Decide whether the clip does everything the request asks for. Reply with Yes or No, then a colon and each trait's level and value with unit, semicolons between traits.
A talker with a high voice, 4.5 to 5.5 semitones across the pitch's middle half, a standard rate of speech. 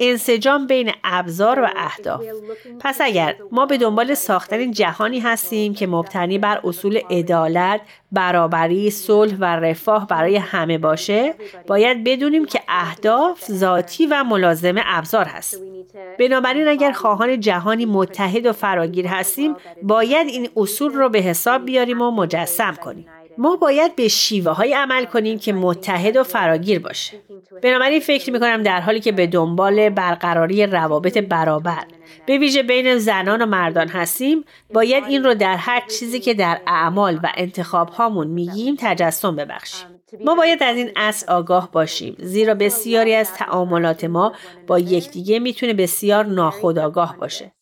Yes: high, 210 Hz; average, 5.1 semitones; average, 145 wpm